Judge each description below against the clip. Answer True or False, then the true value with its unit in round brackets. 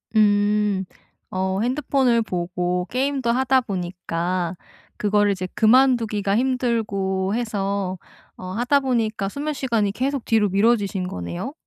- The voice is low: False (210 Hz)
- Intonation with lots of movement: False (4.4 semitones)